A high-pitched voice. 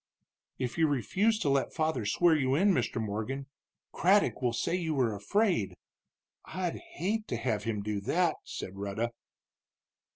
No: low, 135 Hz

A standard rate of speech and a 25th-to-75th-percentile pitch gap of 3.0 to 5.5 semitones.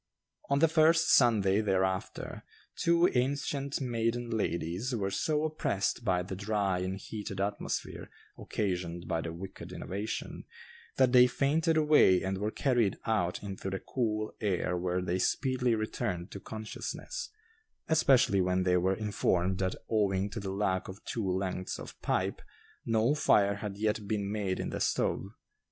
Yes: average, 150 wpm; average, 4.5 semitones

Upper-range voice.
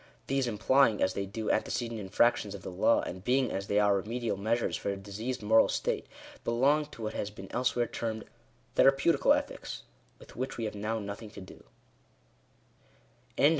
No: low, 110 Hz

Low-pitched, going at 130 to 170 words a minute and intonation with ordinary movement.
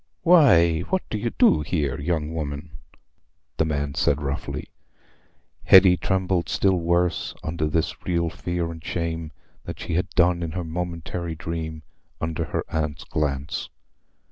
No: very low, 85 Hz; average, 145 wpm; narrow, 2.3 semitones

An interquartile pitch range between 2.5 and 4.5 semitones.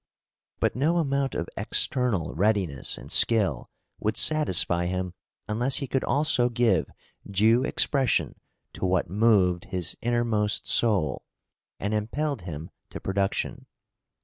No: wide, 5.4 semitones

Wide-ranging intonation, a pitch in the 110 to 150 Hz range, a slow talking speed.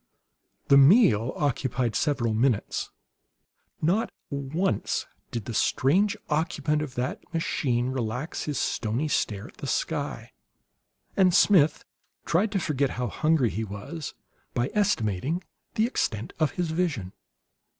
Yes: wide, 5.7 semitones; medium, 140 Hz; slow, 125 wpm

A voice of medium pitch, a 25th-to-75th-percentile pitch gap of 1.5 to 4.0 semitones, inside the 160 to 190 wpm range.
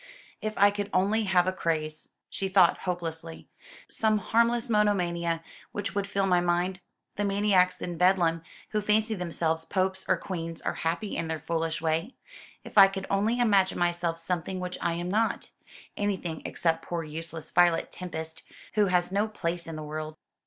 Yes: medium, 180 Hz; average, 3.3 semitones; average, 170 wpm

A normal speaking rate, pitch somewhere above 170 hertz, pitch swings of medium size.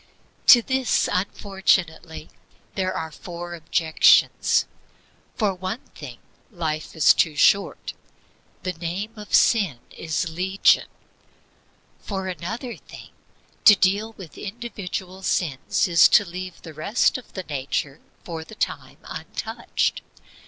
No: slow, 115 wpm; medium, 185 Hz; average, 3.9 semitones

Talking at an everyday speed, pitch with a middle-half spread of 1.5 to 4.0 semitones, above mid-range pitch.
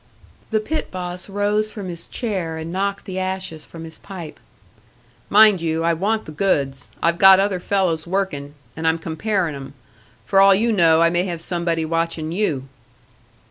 No: average, 175 wpm; average, 3.4 semitones; medium, 175 Hz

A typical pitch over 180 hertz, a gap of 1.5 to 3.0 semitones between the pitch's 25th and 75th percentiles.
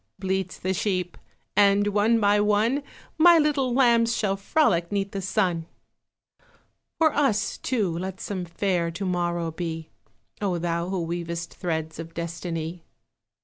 No: high, 190 Hz; average, 3.6 semitones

